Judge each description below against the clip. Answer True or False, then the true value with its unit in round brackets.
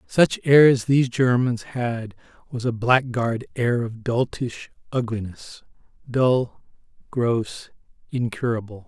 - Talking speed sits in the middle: False (100 wpm)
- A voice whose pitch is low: True (120 Hz)